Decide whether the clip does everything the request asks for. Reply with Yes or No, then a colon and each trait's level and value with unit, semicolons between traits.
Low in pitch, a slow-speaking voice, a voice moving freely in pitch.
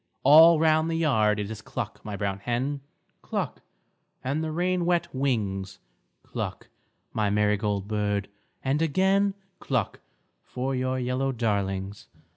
Yes: low, 125 Hz; slow, 130 wpm; wide, 7.0 semitones